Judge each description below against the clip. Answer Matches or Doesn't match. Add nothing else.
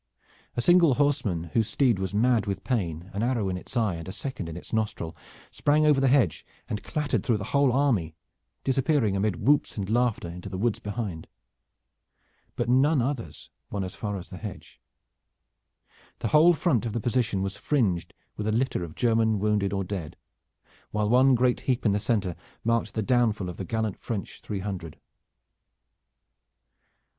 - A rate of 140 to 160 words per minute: Doesn't match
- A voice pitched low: Matches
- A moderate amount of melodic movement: Matches